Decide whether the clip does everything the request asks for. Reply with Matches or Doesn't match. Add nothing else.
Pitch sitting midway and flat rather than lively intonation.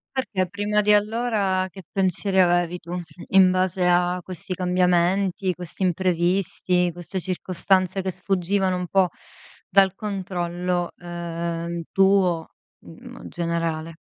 Matches